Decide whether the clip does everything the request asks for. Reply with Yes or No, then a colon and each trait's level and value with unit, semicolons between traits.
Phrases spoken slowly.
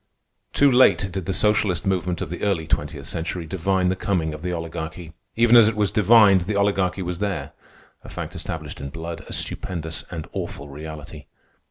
No: average, 180 wpm